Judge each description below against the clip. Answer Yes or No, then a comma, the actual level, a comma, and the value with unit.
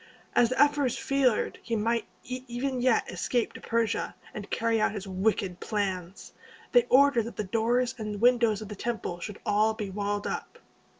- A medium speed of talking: Yes, average, 175 wpm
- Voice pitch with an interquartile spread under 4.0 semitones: Yes, average, 3.0 semitones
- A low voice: No, high, 225 Hz